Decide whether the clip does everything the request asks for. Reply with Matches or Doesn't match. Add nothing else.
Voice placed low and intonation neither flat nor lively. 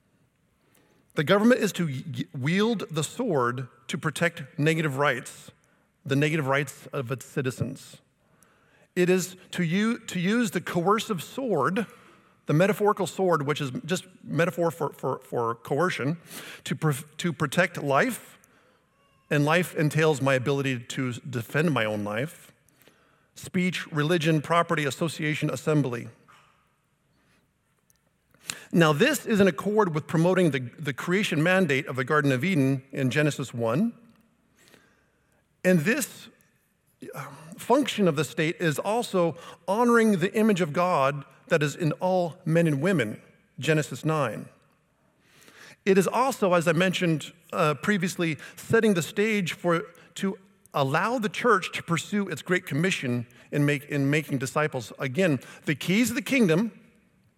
Doesn't match